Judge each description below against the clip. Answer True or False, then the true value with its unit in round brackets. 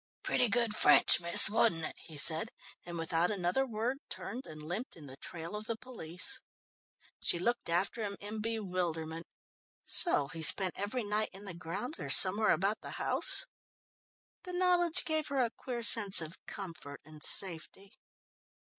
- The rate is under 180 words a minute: True (165 wpm)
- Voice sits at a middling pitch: False (200 Hz)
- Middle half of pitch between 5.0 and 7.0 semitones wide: True (5.6 semitones)